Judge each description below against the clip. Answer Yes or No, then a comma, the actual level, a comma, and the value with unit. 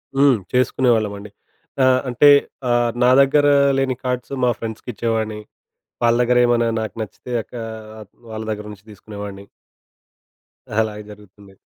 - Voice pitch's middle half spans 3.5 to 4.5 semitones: No, average, 3.0 semitones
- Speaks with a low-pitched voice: Yes, low, 115 Hz